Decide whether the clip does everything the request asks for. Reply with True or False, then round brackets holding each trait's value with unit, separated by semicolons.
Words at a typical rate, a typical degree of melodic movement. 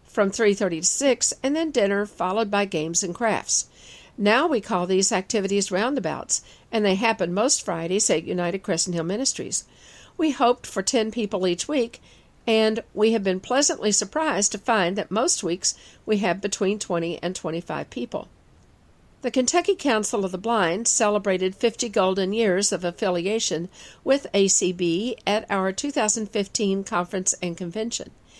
True (155 wpm; 3.8 semitones)